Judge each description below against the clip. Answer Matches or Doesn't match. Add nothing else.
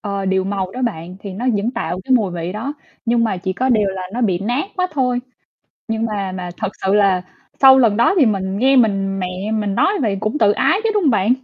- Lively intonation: Doesn't match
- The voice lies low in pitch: Doesn't match